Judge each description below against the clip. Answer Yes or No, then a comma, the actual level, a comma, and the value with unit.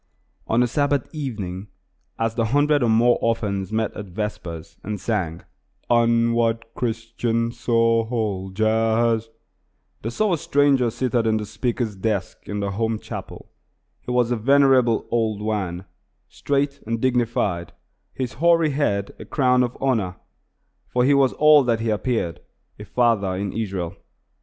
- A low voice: Yes, low, 115 Hz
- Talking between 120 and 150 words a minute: Yes, average, 140 wpm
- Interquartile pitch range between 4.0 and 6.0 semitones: No, average, 3.1 semitones